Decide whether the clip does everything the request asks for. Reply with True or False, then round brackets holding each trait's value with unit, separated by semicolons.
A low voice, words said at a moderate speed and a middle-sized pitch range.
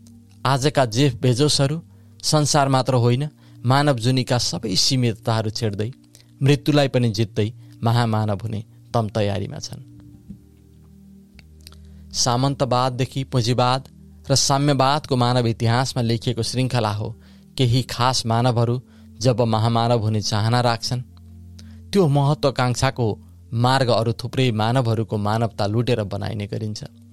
False (120 Hz; 100 wpm; 3.5 semitones)